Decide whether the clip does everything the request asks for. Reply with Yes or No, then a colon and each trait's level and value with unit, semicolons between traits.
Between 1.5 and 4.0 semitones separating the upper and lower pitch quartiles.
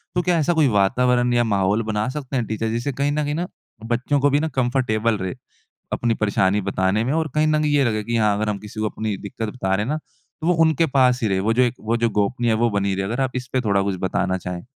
No: average, 4.4 semitones